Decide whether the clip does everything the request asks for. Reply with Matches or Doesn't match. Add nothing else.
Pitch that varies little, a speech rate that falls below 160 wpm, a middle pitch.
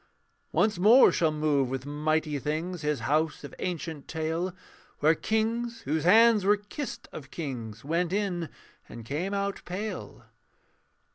Doesn't match